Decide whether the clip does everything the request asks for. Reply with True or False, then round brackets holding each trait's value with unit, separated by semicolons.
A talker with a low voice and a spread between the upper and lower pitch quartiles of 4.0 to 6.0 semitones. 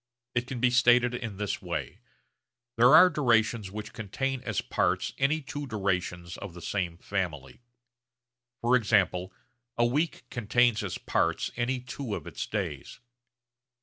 True (115 Hz; 4.4 semitones)